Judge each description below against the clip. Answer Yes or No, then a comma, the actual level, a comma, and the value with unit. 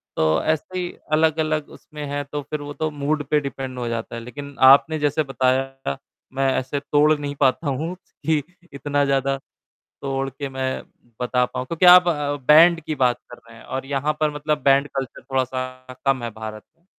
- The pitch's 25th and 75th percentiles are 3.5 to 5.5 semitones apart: No, average, 2.7 semitones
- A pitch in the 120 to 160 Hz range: Yes, medium, 140 Hz